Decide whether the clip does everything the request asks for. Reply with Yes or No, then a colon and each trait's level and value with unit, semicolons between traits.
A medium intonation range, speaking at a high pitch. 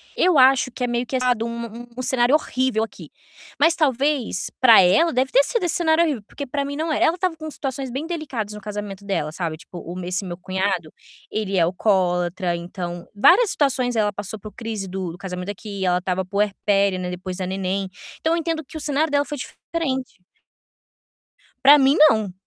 No: wide, 6.9 semitones; high, 225 Hz